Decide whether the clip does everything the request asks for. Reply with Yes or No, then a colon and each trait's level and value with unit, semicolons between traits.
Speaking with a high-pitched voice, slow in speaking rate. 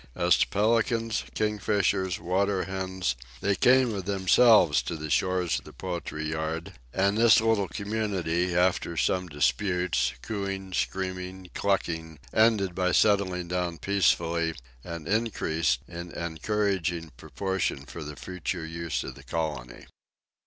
No: very low, 95 Hz; slow, 130 wpm